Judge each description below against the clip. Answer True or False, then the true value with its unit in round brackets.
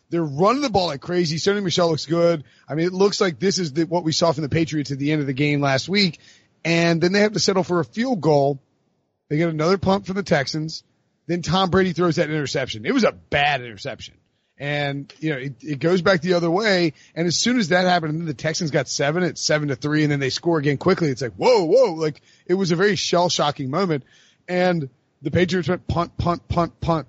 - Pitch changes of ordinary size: True (3.4 semitones)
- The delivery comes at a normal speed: False (250 wpm)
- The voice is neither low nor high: True (170 Hz)